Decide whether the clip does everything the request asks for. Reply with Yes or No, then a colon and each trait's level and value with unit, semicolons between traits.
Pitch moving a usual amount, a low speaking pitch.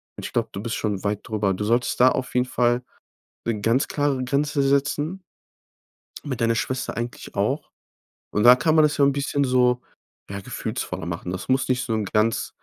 Yes: average, 4.1 semitones; low, 125 Hz